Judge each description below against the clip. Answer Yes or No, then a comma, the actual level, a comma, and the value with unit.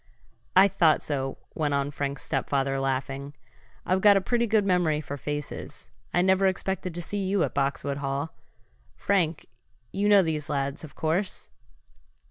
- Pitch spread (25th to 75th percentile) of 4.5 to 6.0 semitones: Yes, average, 5.2 semitones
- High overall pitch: No, medium, 155 Hz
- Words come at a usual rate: Yes, average, 155 wpm